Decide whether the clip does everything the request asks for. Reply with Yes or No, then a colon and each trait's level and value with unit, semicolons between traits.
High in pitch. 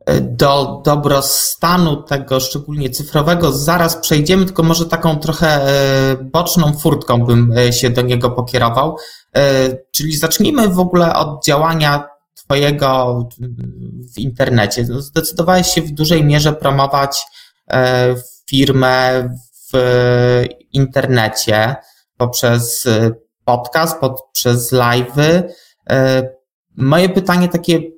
No: low, 135 Hz